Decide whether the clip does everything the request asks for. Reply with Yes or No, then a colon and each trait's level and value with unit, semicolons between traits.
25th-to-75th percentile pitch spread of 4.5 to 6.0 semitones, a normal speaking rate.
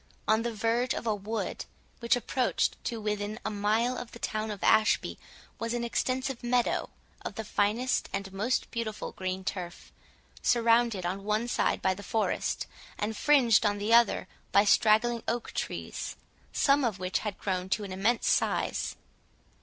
No: narrow, 2.6 semitones; average, 165 wpm